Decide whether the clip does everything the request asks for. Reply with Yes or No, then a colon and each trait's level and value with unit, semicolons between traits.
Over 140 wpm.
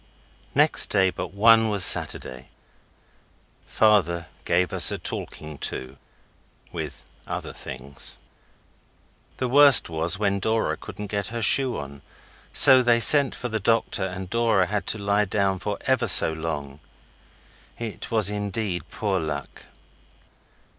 No: slow, 135 wpm